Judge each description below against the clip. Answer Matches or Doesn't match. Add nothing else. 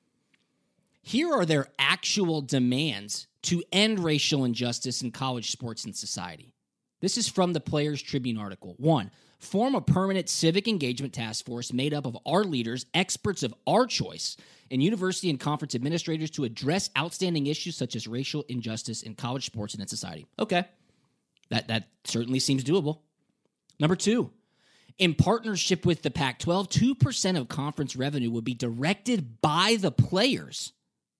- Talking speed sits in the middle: Matches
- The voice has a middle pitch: Matches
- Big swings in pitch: Matches